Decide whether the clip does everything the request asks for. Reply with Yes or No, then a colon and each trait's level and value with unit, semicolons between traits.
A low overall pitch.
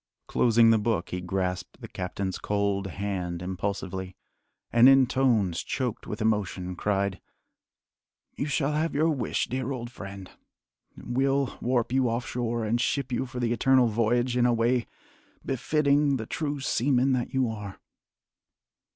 Yes: low, 120 Hz